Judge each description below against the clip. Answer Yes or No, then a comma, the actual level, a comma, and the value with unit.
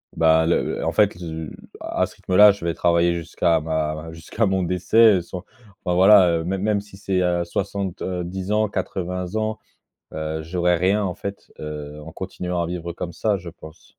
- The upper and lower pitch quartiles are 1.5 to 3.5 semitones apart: Yes, average, 2.8 semitones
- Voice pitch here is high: No, very low, 90 Hz